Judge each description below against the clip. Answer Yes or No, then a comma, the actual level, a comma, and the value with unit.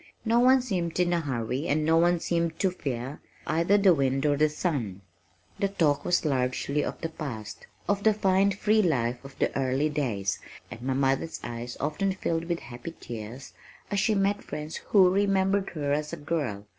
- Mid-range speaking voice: Yes, medium, 155 Hz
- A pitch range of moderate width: No, wide, 6.0 semitones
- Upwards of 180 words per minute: Yes, average, 190 wpm